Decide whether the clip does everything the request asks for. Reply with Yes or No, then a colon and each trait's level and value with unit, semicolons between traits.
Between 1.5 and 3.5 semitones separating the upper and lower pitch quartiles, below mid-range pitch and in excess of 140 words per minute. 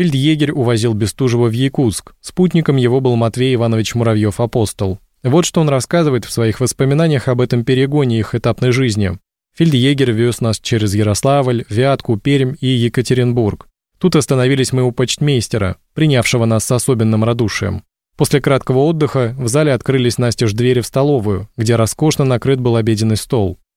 Yes: average, 3.0 semitones; low, 125 Hz; average, 150 wpm